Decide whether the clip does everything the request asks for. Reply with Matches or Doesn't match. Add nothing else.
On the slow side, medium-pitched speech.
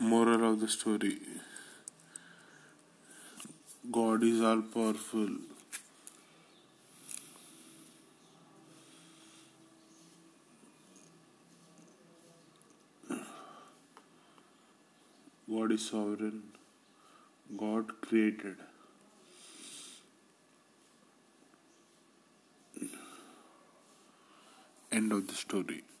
Doesn't match